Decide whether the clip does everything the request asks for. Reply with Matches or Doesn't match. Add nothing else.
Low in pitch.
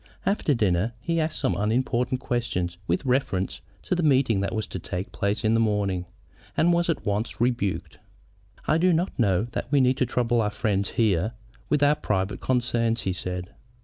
Matches